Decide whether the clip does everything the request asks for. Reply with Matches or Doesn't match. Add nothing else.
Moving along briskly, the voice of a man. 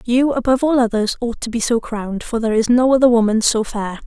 Doesn't match